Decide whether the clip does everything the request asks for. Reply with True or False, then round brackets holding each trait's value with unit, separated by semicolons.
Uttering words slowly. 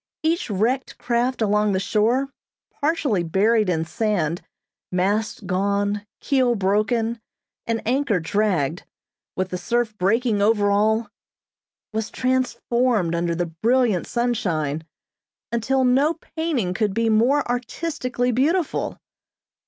True (115 wpm)